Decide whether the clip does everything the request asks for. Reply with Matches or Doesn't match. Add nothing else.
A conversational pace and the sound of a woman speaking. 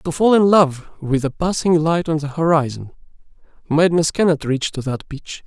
Doesn't match